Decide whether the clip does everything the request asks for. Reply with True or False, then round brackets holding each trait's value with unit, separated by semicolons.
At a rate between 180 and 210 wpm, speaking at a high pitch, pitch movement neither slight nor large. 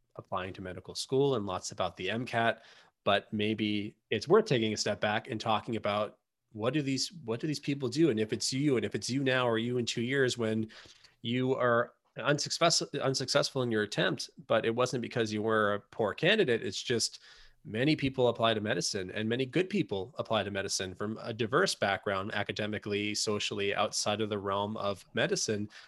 False (195 wpm; 110 Hz; 3.4 semitones)